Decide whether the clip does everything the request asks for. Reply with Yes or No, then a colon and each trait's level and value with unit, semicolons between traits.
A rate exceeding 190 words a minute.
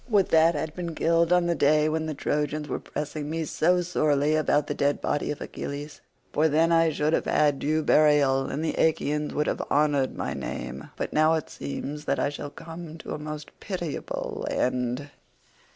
Yes: average, 200 wpm